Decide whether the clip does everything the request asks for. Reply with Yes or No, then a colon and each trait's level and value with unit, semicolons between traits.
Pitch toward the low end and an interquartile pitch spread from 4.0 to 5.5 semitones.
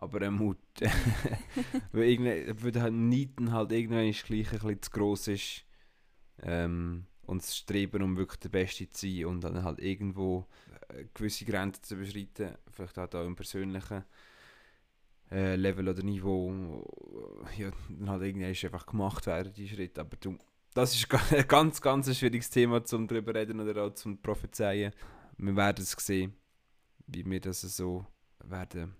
No: low, 100 Hz; average, 3.1 semitones